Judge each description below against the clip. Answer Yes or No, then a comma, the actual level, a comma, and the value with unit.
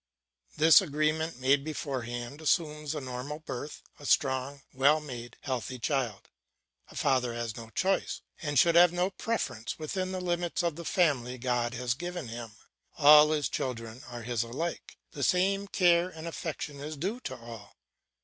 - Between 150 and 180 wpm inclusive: Yes, average, 160 wpm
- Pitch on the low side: No, medium, 145 Hz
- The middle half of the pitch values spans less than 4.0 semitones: No, average, 5.2 semitones